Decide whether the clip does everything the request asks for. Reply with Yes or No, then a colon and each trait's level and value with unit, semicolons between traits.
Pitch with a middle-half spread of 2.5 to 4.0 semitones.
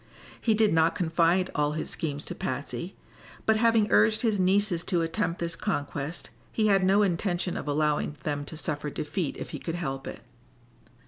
No: average, 5.1 semitones